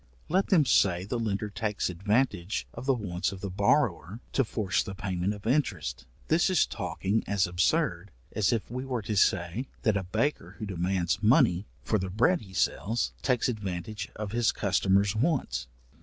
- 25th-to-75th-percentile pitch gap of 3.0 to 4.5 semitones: Yes, average, 4.1 semitones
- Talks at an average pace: Yes, average, 175 wpm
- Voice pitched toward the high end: No, low, 105 Hz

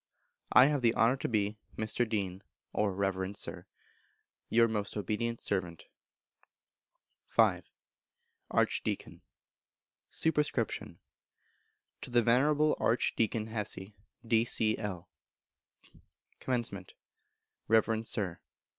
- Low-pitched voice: Yes, low, 110 Hz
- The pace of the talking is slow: Yes, slow, 90 wpm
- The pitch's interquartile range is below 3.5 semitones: Yes, average, 2.8 semitones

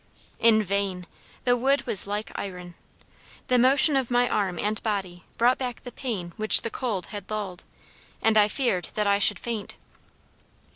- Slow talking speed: No, average, 165 wpm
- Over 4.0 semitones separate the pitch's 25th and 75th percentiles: No, average, 3.6 semitones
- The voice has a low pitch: No, high, 215 Hz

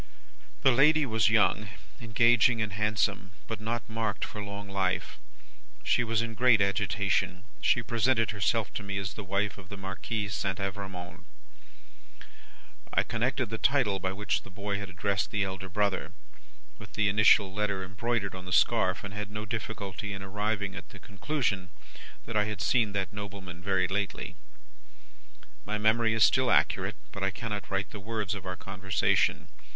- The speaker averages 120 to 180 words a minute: Yes, average, 165 wpm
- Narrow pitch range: Yes, narrow, 2.3 semitones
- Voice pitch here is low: Yes, low, 100 Hz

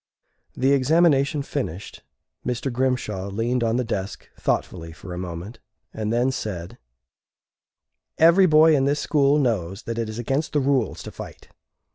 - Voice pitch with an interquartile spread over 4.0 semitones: Yes, average, 5.2 semitones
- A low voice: Yes, low, 125 Hz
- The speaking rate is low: No, average, 150 wpm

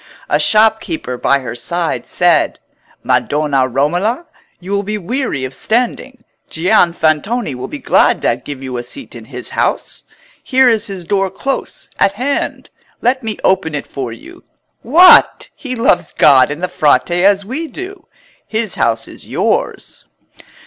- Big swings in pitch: Yes, wide, 8.2 semitones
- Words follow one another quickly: No, average, 155 wpm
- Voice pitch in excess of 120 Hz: Yes, high, 190 Hz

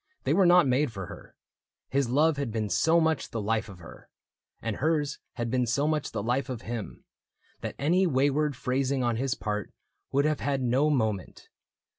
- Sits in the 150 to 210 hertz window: No, low, 135 Hz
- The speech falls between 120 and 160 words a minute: No, average, 190 wpm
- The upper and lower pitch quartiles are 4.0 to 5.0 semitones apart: Yes, average, 4.6 semitones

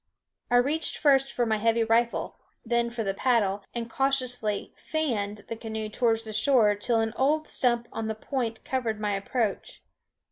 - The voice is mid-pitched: No, high, 230 Hz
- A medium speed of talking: Yes, average, 165 wpm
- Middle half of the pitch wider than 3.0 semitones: No, narrow, 2.6 semitones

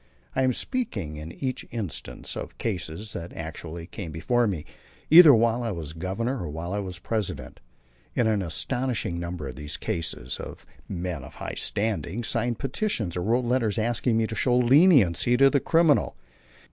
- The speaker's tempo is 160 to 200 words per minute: Yes, average, 170 wpm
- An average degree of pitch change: No, wide, 6.2 semitones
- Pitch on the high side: No, low, 110 Hz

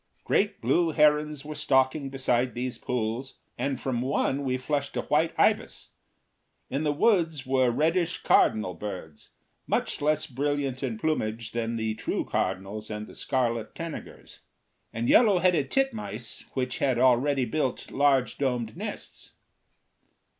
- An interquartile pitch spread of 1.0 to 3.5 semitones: No, average, 4.2 semitones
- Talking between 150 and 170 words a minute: No, average, 140 wpm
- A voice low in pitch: Yes, low, 130 Hz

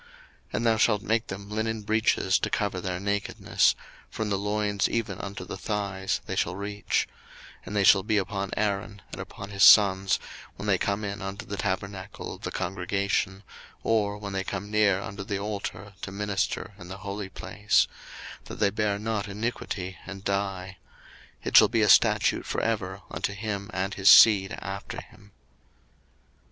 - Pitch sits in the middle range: No, low, 100 Hz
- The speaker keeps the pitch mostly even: Yes, narrow, 1.4 semitones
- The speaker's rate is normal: Yes, average, 175 wpm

